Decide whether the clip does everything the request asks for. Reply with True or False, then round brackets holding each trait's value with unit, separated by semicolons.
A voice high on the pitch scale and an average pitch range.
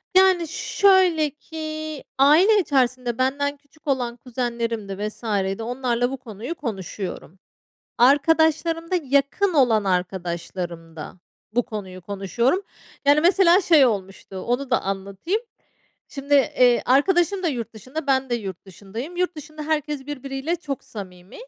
False (265 Hz; 6.4 semitones)